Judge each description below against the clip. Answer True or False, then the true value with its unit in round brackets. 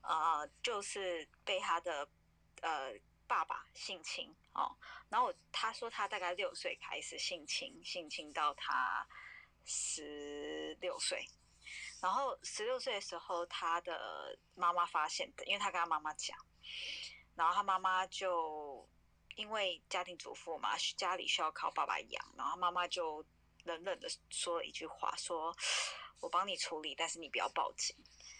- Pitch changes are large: True (5.7 semitones)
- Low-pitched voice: False (180 Hz)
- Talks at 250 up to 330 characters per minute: False (220 characters per minute)